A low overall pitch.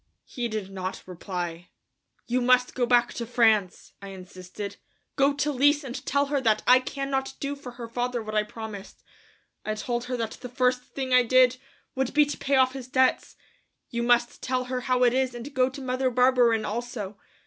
No: high, 245 Hz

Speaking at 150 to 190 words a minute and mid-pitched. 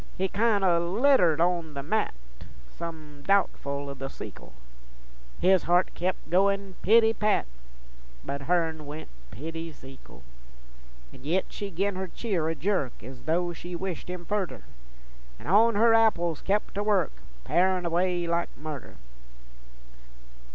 No: average, 140 wpm; medium, 175 Hz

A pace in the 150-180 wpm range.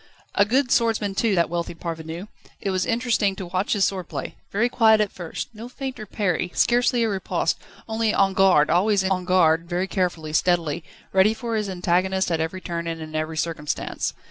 No: average, 195 wpm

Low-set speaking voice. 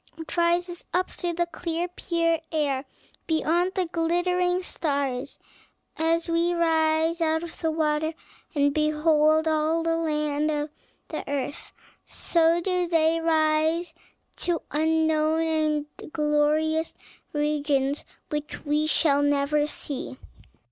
No: very high, 315 Hz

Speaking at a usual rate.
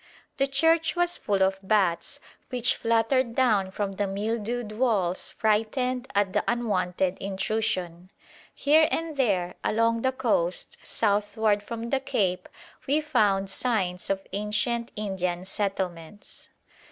No: slow, 125 wpm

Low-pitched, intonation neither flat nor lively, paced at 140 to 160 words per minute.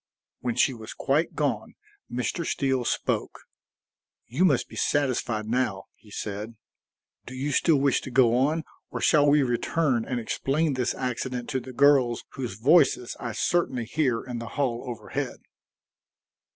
Yes: low, 130 Hz; average, 3.1 semitones; average, 150 wpm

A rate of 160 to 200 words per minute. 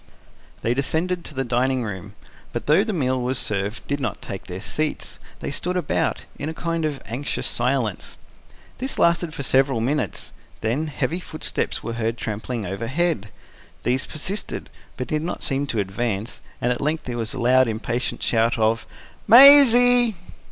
Yes: average, 165 wpm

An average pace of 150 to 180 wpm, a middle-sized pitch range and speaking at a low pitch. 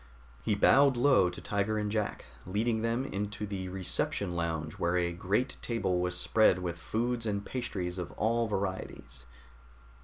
Yes: average, 155 wpm; average, 4.1 semitones; low, 100 Hz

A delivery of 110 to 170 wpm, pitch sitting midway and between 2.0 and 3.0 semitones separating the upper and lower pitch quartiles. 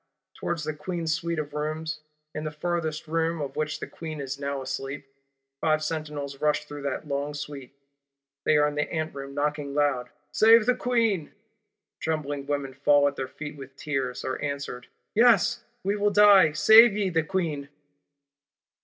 Yes: average, 165 wpm; medium, 150 Hz; average, 2.7 semitones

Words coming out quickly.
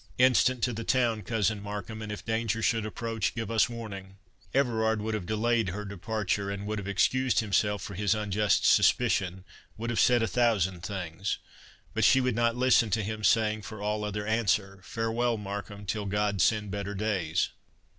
No: average, 175 wpm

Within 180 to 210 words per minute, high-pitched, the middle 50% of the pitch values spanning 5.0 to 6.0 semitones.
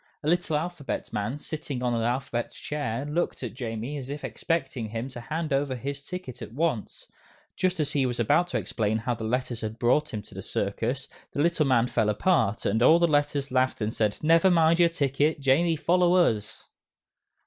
No: average, 200 wpm; low, 135 Hz; average, 5.3 semitones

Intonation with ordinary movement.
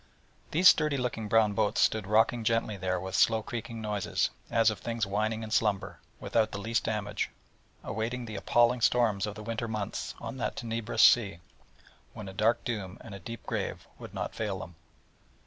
No: narrow, 2.2 semitones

